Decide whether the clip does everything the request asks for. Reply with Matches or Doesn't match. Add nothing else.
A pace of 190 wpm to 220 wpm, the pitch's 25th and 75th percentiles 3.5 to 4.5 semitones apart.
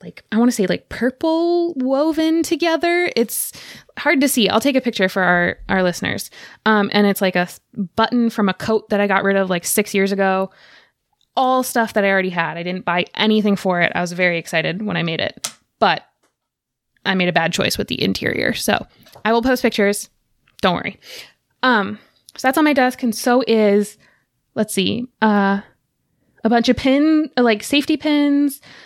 Doesn't match